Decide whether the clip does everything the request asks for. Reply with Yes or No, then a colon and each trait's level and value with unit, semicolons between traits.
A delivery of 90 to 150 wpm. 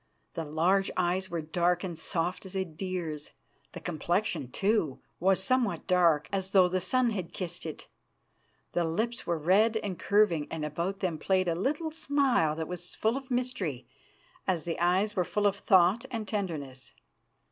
No: average, 170 wpm